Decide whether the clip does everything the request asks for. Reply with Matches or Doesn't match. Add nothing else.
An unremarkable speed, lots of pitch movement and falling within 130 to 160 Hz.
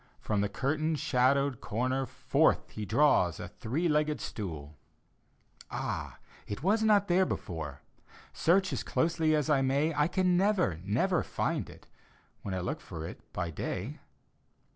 Matches